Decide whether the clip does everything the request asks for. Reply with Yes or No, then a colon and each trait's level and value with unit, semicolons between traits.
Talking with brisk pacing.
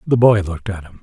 Yes: fast, 295 wpm